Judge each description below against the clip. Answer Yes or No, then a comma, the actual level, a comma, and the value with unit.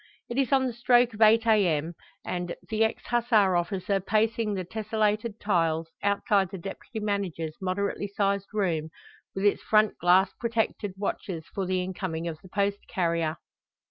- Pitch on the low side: No, high, 200 Hz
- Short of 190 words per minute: Yes, average, 160 wpm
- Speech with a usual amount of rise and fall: Yes, average, 3.5 semitones